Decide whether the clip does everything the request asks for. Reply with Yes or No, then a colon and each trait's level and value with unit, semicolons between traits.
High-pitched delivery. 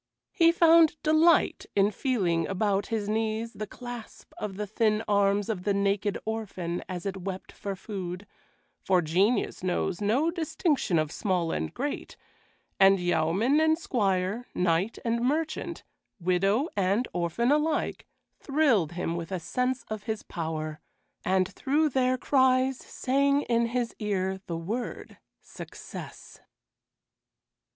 Yes: high, 210 Hz